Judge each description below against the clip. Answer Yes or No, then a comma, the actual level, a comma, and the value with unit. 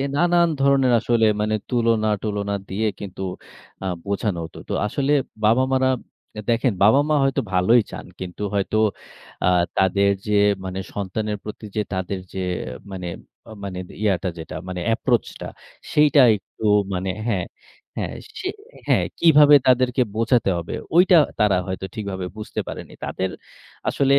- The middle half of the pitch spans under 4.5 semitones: No, average, 5.3 semitones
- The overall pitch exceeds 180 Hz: No, low, 110 Hz